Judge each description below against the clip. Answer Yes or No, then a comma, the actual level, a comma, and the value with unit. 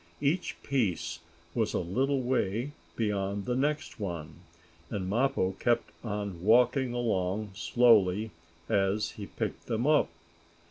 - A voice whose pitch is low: Yes, low, 110 Hz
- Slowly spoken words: Yes, slow, 125 wpm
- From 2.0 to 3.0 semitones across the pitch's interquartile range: No, average, 4.4 semitones